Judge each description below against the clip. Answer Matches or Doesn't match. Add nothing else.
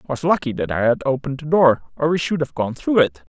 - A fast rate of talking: Matches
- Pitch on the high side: Doesn't match